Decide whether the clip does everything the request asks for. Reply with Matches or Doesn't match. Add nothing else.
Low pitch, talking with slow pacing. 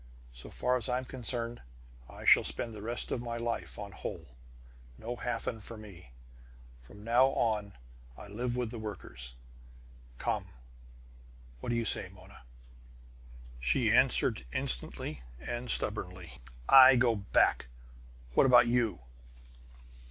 Matches